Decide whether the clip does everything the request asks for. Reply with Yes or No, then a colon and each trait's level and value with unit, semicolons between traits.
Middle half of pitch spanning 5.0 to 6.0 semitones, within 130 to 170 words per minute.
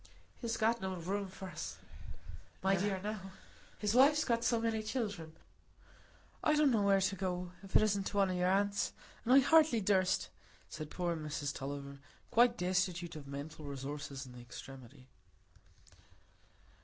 Yes: wide, 5.5 semitones; average, 160 wpm